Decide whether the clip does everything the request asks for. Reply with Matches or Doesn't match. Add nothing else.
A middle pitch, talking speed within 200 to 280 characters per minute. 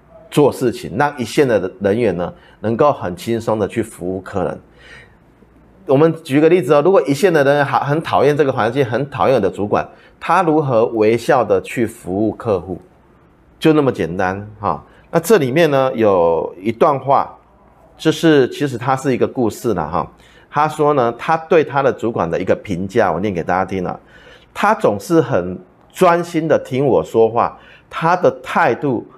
Matches